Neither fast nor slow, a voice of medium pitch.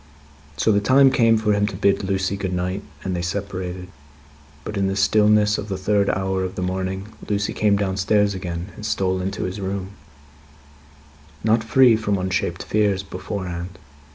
No: average, 170 wpm; low, 100 Hz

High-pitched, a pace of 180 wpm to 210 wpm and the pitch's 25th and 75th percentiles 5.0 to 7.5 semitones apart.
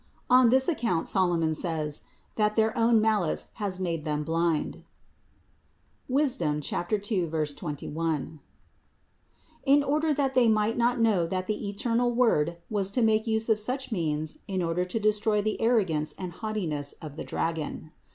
No: high, 200 Hz; average, 150 wpm; wide, 5.6 semitones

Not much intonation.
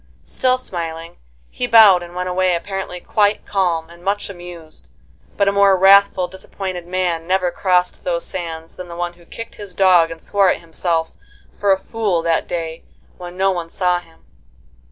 Yes: narrow, 2.2 semitones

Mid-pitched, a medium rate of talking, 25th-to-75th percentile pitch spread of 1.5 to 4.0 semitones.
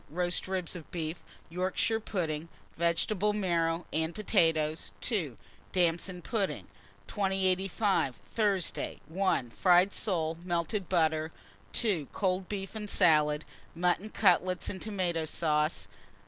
No: medium, 180 Hz; slow, 110 wpm; average, 3.1 semitones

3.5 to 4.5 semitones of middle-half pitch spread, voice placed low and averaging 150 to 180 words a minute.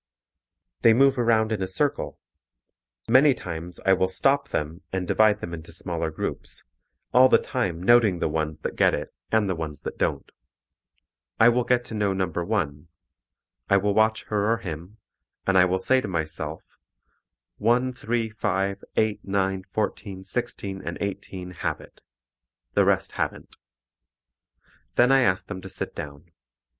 Yes: average, 4.0 semitones; low, 100 Hz; average, 160 wpm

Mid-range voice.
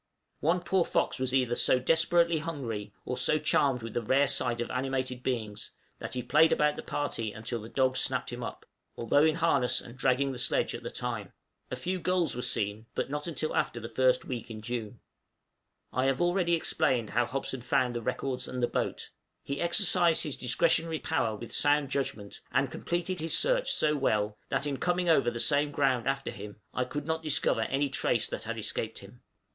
No: low, 130 Hz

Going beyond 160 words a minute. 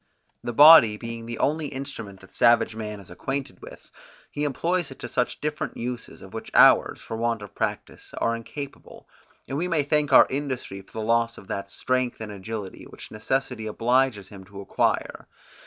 Yes: average, 180 wpm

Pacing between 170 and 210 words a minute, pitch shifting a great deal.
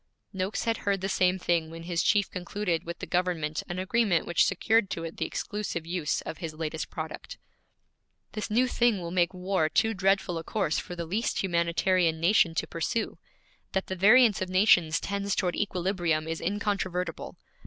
No: average, 180 wpm; average, 3.2 semitones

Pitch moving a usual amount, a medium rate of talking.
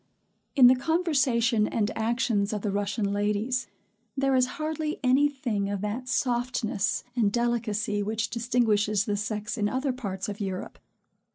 Yes: average, 3.6 semitones; average, 150 wpm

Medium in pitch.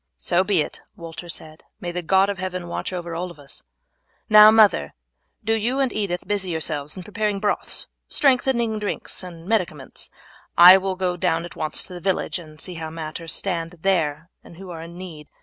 Yes: medium, 180 Hz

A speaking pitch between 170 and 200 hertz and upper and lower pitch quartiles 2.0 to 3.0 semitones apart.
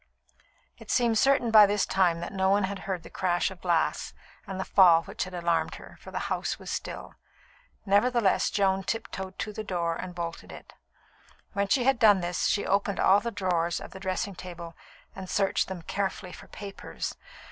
Yes: high, 190 Hz; narrow, 2.5 semitones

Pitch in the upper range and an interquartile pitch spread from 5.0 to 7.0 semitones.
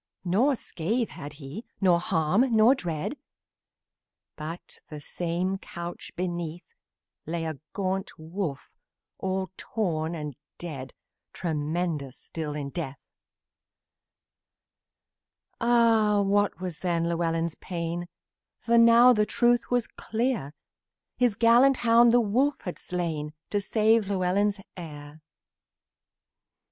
No: medium, 180 Hz; wide, 5.4 semitones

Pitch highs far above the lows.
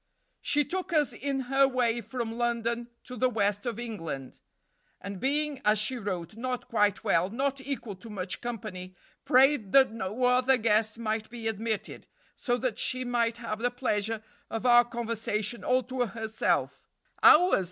No: average, 3.0 semitones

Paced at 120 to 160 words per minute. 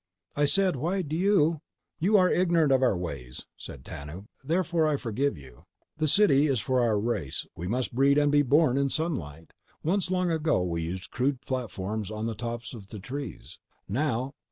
No: average, 180 wpm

